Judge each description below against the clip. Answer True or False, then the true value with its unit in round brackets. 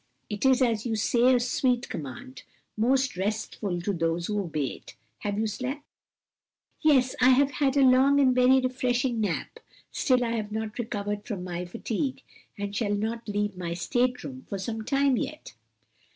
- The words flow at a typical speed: True (175 wpm)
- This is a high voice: True (230 Hz)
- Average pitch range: True (4.0 semitones)